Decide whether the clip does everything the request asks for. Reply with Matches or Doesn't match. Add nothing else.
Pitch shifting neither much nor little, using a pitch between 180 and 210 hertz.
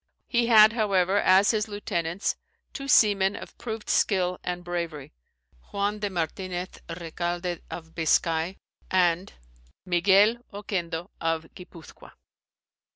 Matches